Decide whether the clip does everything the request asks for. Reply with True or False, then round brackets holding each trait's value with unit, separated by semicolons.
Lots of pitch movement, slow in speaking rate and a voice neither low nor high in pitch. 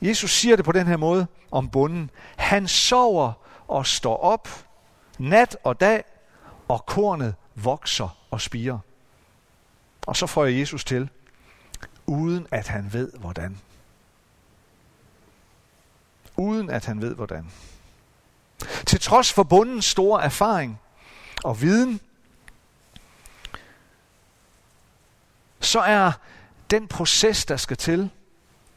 True (8.5 semitones; 110 wpm; 150 Hz)